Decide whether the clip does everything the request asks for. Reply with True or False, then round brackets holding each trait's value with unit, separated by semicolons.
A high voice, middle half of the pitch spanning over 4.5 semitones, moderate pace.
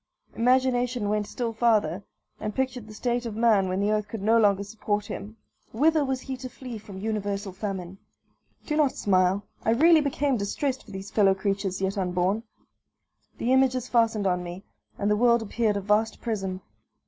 False (215 Hz; 3.6 semitones; 180 wpm)